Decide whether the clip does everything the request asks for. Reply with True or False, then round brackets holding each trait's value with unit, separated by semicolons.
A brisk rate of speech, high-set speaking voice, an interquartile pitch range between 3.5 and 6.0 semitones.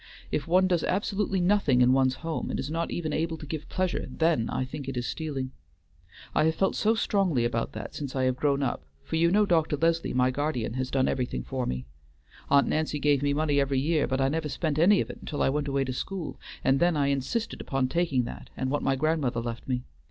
False (235 wpm; 145 Hz; 4.0 semitones)